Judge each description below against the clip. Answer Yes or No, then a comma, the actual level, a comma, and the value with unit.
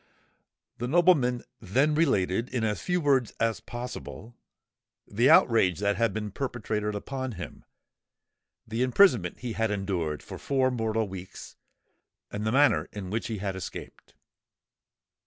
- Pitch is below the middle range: Yes, low, 115 Hz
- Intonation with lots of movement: No, average, 4.0 semitones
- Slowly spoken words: Yes, slow, 130 wpm